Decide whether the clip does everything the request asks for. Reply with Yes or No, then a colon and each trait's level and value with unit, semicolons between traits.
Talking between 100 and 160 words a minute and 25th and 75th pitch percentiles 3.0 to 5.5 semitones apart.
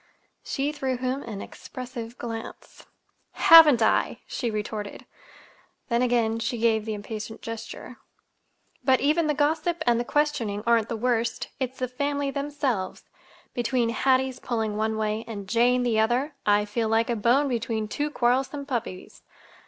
Yes: average, 150 wpm; average, 3.3 semitones